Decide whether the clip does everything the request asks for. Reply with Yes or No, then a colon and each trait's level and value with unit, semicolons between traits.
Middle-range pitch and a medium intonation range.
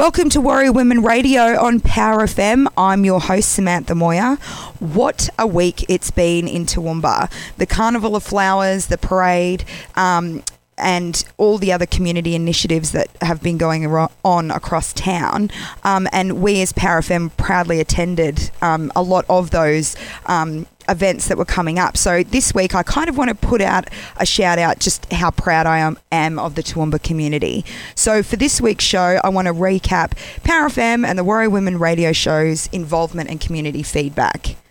Yes: medium, 180 Hz; average, 3.5 semitones